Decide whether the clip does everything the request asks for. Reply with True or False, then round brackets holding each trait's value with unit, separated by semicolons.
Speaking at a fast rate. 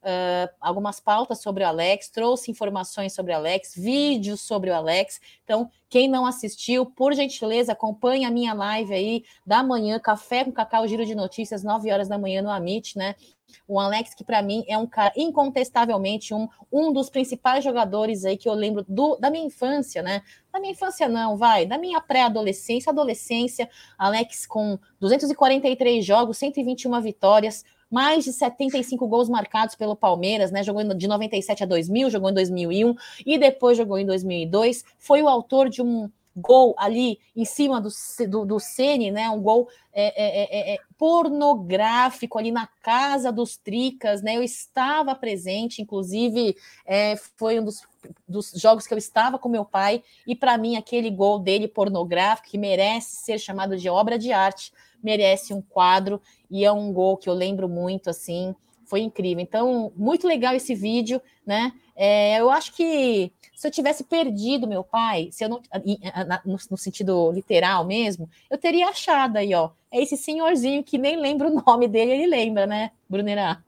False (175 wpm)